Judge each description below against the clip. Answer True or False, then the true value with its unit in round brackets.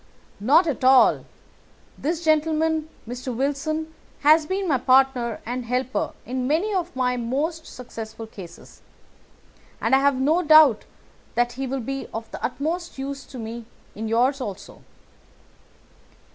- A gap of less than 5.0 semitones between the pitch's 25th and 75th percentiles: True (4.2 semitones)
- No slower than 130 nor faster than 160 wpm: True (140 wpm)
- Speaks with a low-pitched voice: False (270 Hz)